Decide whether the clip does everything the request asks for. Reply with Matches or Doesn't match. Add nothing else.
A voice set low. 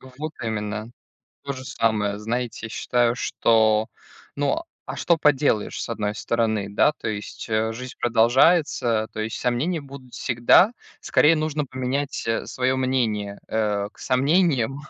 Matches